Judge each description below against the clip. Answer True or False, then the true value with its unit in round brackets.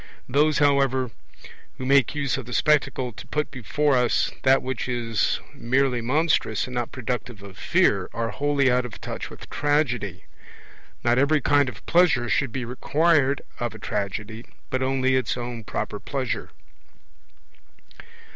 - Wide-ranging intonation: False (2.9 semitones)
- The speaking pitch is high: False (130 Hz)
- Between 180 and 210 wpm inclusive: False (150 wpm)